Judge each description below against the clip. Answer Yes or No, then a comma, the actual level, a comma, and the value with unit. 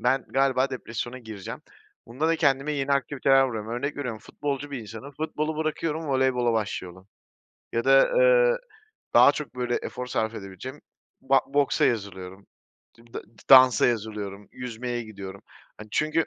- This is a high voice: No, low, 125 Hz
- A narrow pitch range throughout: No, average, 4.2 semitones